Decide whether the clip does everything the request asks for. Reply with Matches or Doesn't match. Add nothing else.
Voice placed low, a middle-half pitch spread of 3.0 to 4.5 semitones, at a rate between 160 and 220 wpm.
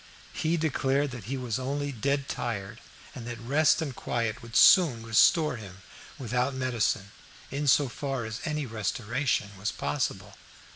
Doesn't match